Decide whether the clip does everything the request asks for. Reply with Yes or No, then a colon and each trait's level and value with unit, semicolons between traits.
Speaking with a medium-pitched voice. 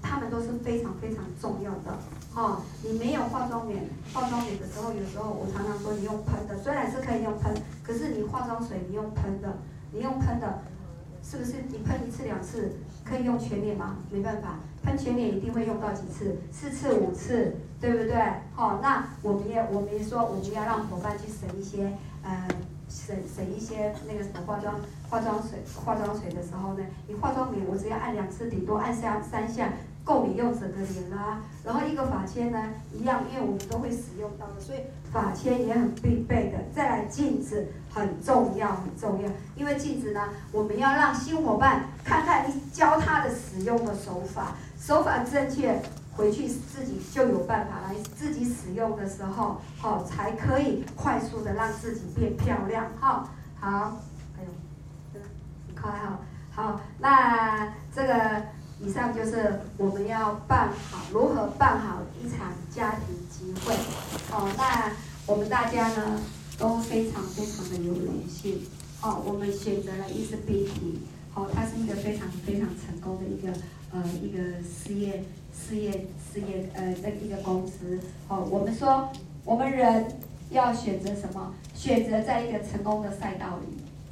No: high, 210 Hz